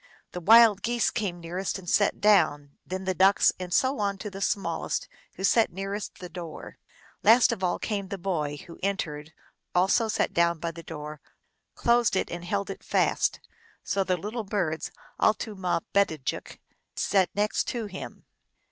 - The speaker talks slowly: No, average, 170 wpm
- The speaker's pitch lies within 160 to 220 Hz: Yes, high, 190 Hz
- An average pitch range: Yes, average, 3.3 semitones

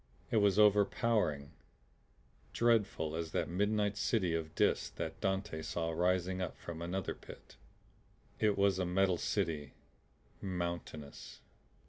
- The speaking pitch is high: No, very low, 90 Hz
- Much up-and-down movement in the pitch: No, average, 3.7 semitones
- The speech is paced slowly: Yes, slow, 120 wpm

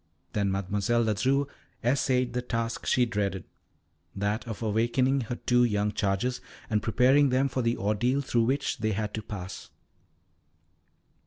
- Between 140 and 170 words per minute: Yes, average, 145 wpm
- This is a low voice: Yes, low, 115 Hz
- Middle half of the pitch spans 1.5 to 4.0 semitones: Yes, average, 3.3 semitones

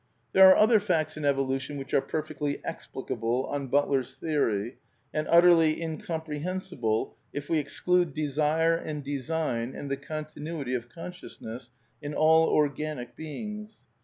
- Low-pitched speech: No, medium, 150 Hz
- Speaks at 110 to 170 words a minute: Yes, average, 140 wpm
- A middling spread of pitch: Yes, average, 3.3 semitones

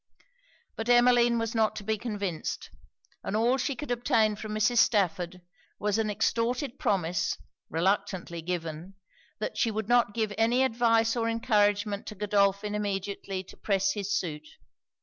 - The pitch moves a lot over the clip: No, average, 2.8 semitones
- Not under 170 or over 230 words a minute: No, average, 150 wpm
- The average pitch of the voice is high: Yes, high, 210 Hz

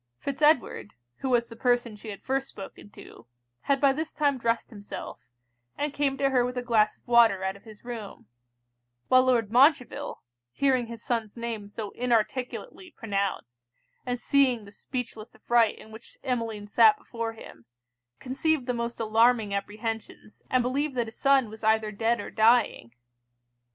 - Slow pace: No, average, 165 wpm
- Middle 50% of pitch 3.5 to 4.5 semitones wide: No, average, 3.1 semitones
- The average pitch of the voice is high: Yes, high, 235 Hz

